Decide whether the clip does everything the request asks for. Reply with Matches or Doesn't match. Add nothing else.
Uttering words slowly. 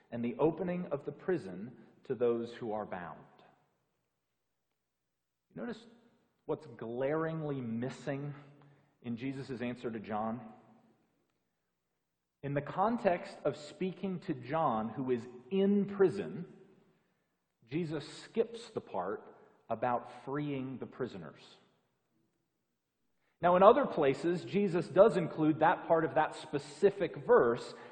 Matches